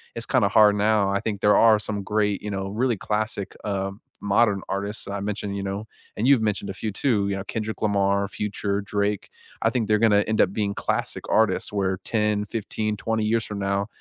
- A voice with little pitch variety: Yes, narrow, 1.5 semitones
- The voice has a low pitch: Yes, low, 105 Hz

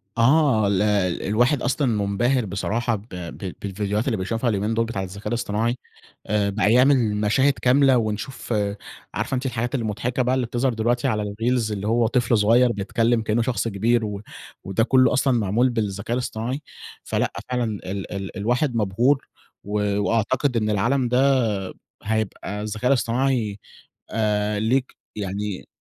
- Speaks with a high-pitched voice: No, low, 115 Hz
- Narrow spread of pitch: No, average, 3.1 semitones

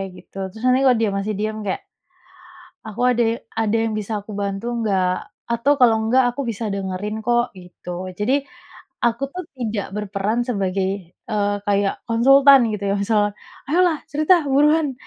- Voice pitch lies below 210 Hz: No, high, 220 Hz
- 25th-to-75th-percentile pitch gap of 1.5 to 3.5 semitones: No, average, 4.1 semitones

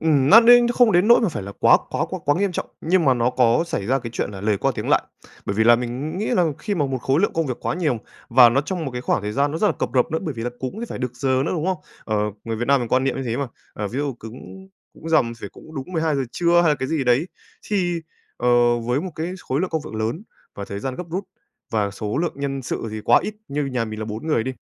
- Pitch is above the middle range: No, low, 135 Hz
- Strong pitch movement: Yes, wide, 5.7 semitones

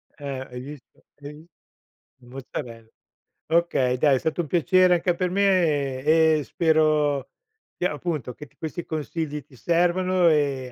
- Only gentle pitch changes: No, average, 3.9 semitones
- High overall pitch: No, medium, 155 Hz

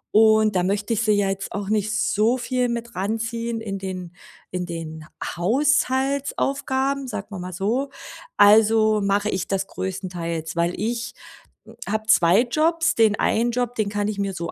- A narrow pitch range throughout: No, average, 3.6 semitones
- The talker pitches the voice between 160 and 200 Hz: No, high, 215 Hz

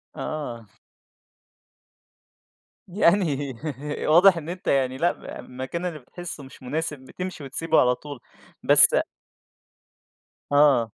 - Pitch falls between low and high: Yes, medium, 150 Hz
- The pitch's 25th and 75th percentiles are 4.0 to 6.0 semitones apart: Yes, average, 4.5 semitones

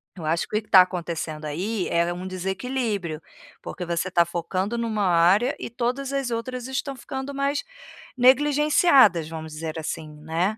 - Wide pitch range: Yes, wide, 7.1 semitones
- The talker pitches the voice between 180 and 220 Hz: Yes, high, 190 Hz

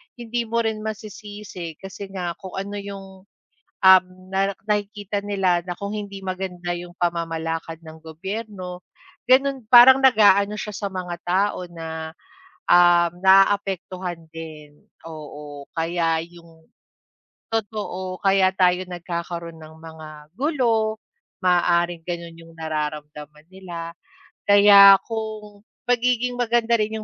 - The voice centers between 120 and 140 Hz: No, medium, 185 Hz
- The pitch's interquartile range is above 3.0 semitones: Yes, average, 3.7 semitones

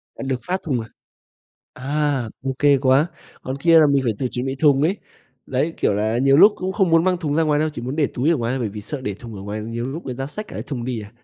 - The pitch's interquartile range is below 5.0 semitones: Yes, average, 4.2 semitones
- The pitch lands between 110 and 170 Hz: Yes, low, 135 Hz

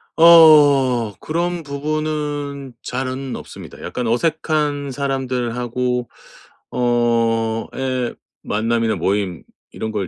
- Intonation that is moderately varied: Yes, average, 3.8 semitones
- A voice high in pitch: No, low, 130 Hz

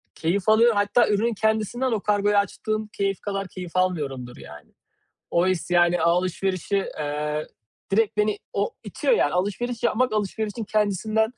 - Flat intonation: No, average, 3.5 semitones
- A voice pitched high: Yes, high, 200 Hz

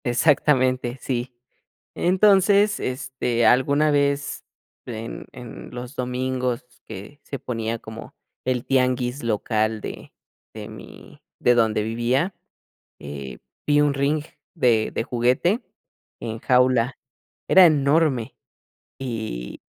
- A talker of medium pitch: No, low, 125 Hz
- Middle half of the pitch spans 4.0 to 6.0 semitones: No, average, 3.6 semitones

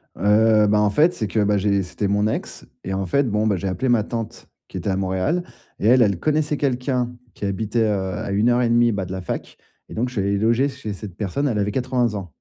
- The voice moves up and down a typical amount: Yes, average, 3.6 semitones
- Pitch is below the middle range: Yes, low, 105 Hz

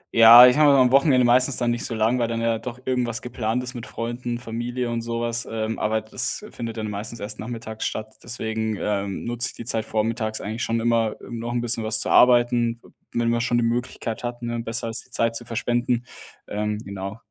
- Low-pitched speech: Yes, low, 115 Hz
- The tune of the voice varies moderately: No, narrow, 1.5 semitones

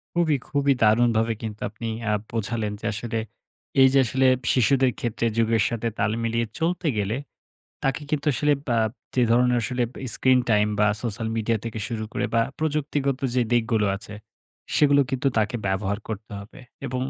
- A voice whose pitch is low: Yes, low, 115 Hz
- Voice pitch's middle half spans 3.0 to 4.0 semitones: Yes, average, 3.3 semitones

